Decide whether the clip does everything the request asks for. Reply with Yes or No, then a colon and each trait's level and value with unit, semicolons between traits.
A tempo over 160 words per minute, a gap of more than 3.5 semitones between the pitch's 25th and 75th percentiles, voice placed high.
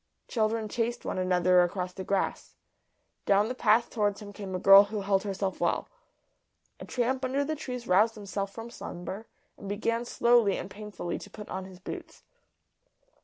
No: average, 170 wpm; average, 3.2 semitones; high, 205 Hz